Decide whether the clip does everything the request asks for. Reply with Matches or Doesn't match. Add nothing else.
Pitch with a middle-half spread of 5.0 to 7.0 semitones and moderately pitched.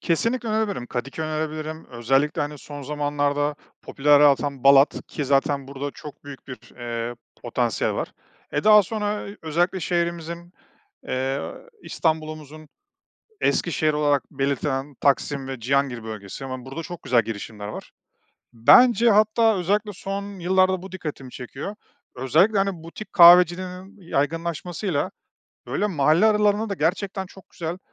Matches